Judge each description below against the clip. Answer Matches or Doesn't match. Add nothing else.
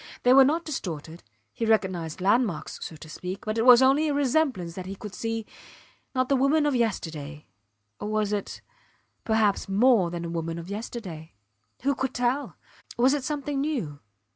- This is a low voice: Doesn't match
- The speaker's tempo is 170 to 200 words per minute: Matches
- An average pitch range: Doesn't match